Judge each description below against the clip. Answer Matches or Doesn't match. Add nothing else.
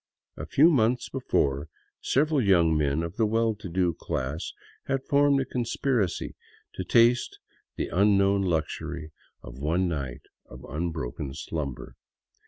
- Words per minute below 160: Matches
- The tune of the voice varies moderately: Doesn't match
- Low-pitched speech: Matches